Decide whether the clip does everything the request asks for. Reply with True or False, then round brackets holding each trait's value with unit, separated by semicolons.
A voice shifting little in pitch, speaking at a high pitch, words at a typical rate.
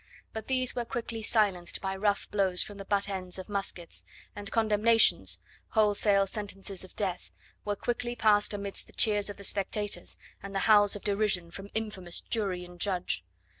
True (1.9 semitones; 205 Hz; 170 wpm)